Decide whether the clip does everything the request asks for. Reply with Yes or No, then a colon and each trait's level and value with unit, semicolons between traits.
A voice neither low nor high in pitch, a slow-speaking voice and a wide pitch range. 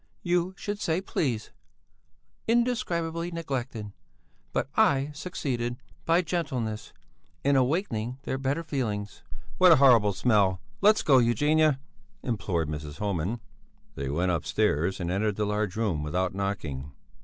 No: low, 120 Hz; slow, 125 wpm; wide, 8.5 semitones